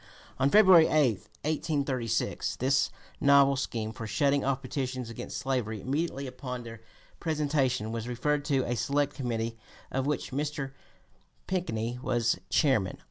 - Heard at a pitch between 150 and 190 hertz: No, low, 130 Hz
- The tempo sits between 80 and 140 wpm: Yes, slow, 135 wpm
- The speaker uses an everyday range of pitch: Yes, average, 3.5 semitones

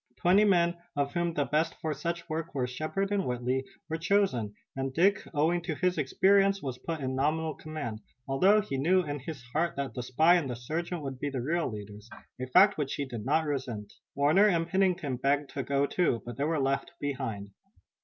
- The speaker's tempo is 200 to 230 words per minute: Yes, fast, 205 wpm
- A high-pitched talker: No, medium, 150 Hz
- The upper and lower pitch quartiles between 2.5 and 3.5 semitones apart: No, average, 4.6 semitones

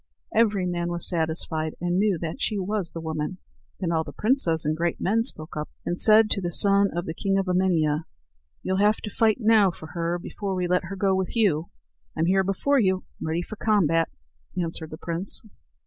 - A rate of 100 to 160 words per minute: No, fast, 205 wpm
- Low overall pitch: No, medium, 180 Hz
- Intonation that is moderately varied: Yes, average, 3.4 semitones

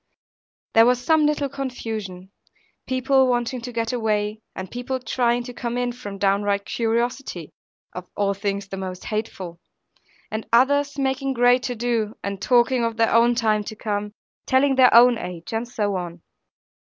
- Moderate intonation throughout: Yes, average, 3.5 semitones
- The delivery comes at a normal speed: Yes, average, 165 wpm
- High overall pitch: Yes, high, 230 Hz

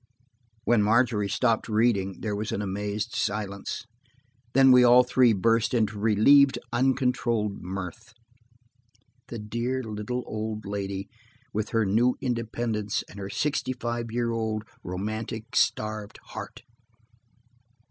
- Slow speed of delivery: Yes, slow, 120 wpm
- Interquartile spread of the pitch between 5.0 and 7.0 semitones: No, narrow, 2.6 semitones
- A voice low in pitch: Yes, low, 110 Hz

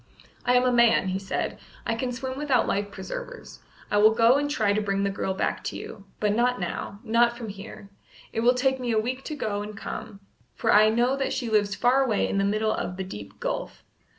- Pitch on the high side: Yes, high, 225 Hz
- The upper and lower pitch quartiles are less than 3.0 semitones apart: No, average, 3.6 semitones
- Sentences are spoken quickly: Yes, fast, 235 wpm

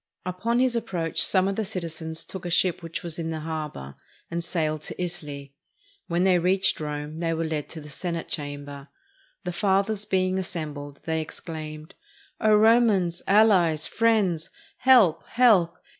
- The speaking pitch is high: No, medium, 170 Hz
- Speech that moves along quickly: No, average, 160 wpm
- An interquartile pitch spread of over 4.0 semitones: No, average, 3.6 semitones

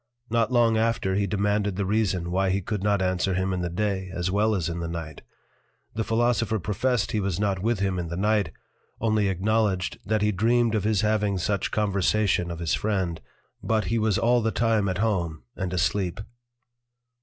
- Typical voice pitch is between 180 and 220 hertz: No, low, 100 Hz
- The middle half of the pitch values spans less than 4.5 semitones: Yes, average, 2.8 semitones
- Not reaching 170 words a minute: No, average, 195 wpm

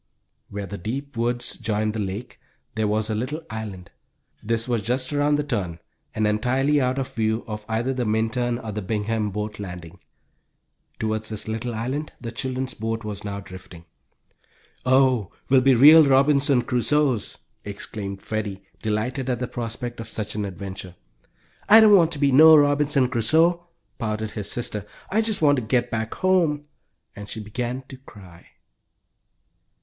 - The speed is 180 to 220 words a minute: No, average, 165 wpm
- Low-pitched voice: Yes, low, 115 Hz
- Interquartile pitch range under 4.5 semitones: Yes, average, 3.9 semitones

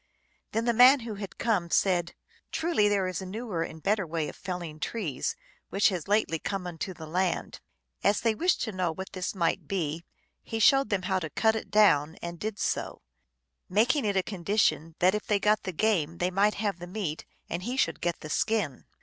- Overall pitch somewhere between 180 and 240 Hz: Yes, high, 190 Hz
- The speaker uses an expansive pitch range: No, average, 3.9 semitones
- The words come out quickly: Yes, fast, 210 wpm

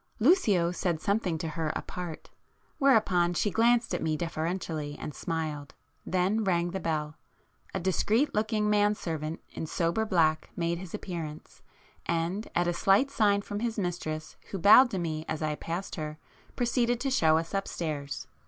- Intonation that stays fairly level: No, average, 4.7 semitones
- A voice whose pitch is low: No, medium, 175 Hz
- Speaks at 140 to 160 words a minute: Yes, average, 155 wpm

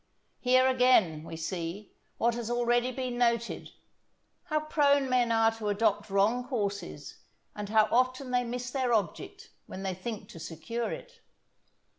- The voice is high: Yes, high, 235 Hz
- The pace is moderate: Yes, average, 150 wpm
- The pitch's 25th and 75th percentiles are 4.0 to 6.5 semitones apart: No, average, 3.6 semitones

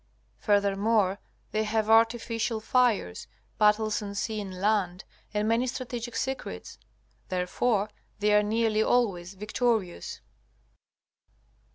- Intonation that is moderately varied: No, narrow, 2.3 semitones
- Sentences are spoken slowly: Yes, slow, 100 wpm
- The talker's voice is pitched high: Yes, high, 215 Hz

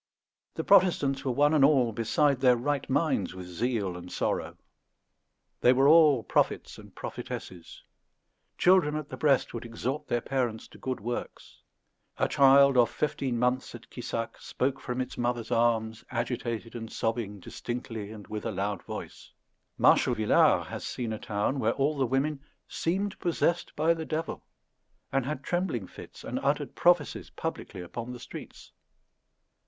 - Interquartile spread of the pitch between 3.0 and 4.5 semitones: Yes, average, 3.9 semitones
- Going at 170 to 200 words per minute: No, average, 160 wpm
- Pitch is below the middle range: Yes, low, 125 Hz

